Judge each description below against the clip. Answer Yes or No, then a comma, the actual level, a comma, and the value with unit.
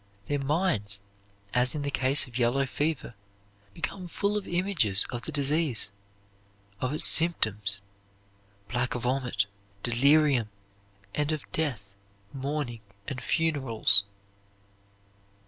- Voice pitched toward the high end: No, low, 135 Hz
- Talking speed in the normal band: No, slow, 110 wpm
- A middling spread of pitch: Yes, average, 4.5 semitones